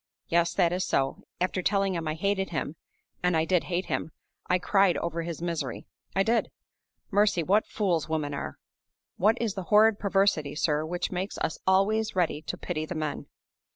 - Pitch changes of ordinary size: Yes, average, 3.4 semitones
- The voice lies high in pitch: No, medium, 180 Hz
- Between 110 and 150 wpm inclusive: No, average, 185 wpm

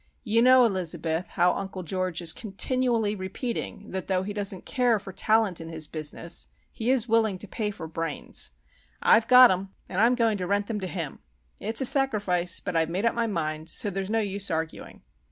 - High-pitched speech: Yes, high, 195 Hz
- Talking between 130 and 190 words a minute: No, average, 200 wpm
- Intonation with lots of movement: No, average, 4.1 semitones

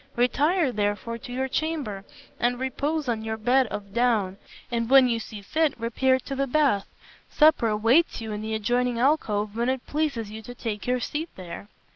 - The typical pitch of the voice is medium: No, high, 240 Hz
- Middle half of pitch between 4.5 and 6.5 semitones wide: No, average, 3.7 semitones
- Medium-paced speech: Yes, average, 185 wpm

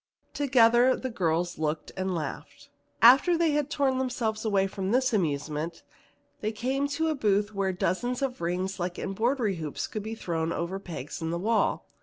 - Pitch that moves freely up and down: Yes, wide, 6.4 semitones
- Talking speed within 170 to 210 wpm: Yes, average, 175 wpm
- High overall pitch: Yes, high, 210 Hz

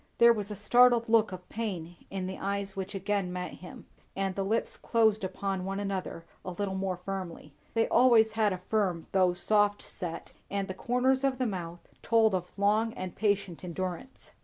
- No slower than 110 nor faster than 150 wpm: No, average, 185 wpm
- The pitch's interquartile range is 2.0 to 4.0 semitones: Yes, average, 3.1 semitones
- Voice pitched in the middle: No, high, 195 Hz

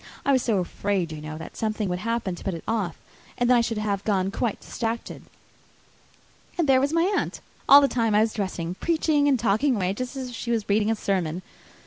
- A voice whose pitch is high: Yes, high, 220 Hz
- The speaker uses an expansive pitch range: No, average, 4.7 semitones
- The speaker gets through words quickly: Yes, fast, 225 wpm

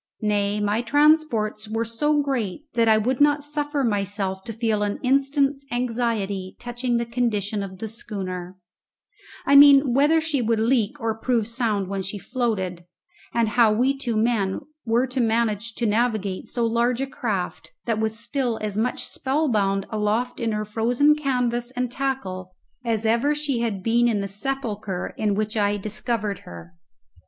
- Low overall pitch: No, high, 230 Hz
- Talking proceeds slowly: No, average, 165 wpm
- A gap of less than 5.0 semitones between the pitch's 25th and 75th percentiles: Yes, average, 3.4 semitones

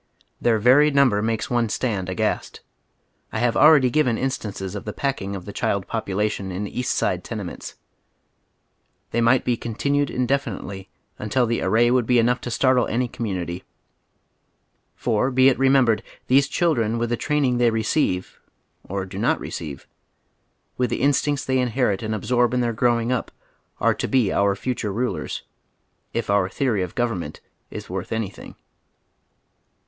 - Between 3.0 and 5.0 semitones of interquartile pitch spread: Yes, average, 3.8 semitones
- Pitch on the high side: No, low, 115 Hz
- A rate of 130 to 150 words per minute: No, average, 160 wpm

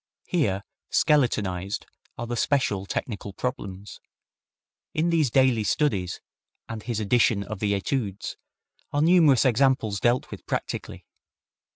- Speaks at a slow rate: Yes, slow, 115 wpm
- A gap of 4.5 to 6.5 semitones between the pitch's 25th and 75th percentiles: Yes, average, 5.1 semitones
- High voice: No, low, 115 Hz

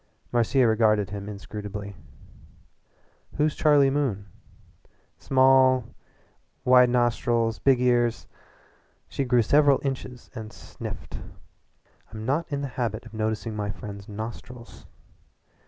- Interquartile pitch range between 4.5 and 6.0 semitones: No, average, 3.5 semitones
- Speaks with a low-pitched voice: Yes, low, 120 Hz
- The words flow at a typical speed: No, slow, 105 wpm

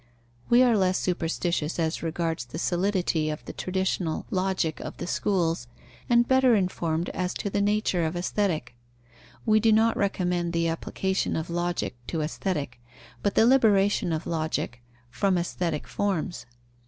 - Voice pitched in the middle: Yes, medium, 180 Hz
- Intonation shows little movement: No, average, 3.6 semitones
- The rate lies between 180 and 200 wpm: No, average, 150 wpm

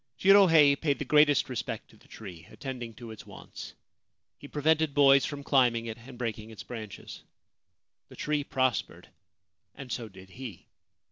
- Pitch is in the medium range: No, low, 130 Hz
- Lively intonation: No, average, 4.2 semitones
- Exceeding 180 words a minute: No, average, 155 wpm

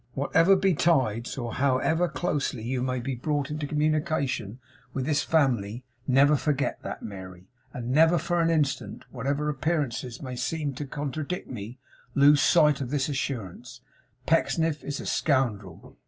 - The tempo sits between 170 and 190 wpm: No, average, 145 wpm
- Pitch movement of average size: Yes, average, 3.6 semitones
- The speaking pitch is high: No, medium, 140 Hz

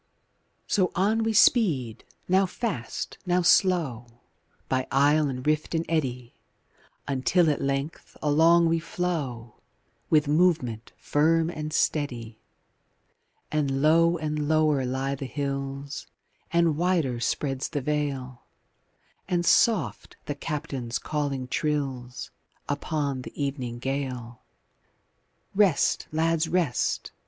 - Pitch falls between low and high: Yes, medium, 150 Hz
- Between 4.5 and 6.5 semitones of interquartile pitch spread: No, average, 3.9 semitones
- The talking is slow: Yes, slow, 110 wpm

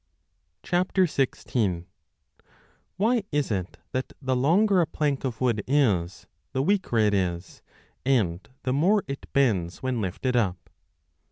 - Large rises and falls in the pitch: Yes, wide, 6.6 semitones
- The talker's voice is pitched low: Yes, low, 130 Hz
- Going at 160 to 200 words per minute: No, slow, 135 wpm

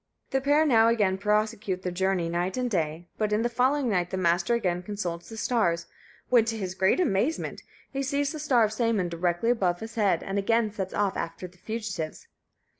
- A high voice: Yes, high, 210 Hz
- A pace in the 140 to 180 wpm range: No, average, 200 wpm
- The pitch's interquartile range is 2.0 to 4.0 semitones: No, average, 4.5 semitones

